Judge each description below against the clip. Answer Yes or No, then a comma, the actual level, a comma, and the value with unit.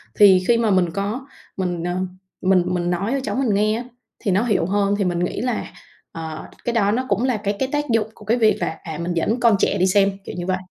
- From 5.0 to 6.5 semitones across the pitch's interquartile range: No, average, 4.0 semitones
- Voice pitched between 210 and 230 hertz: No, high, 200 Hz